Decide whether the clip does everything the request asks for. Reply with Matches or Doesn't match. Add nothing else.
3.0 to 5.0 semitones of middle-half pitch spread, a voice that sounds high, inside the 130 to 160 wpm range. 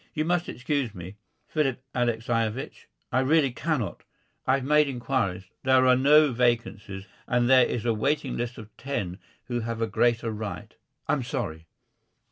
Doesn't match